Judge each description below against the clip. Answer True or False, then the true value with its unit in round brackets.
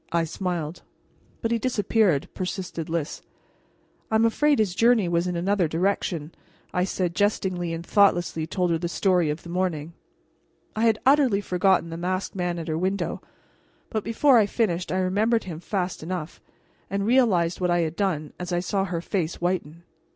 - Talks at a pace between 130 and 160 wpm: False (175 wpm)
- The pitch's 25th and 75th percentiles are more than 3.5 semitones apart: False (3.2 semitones)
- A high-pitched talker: False (180 Hz)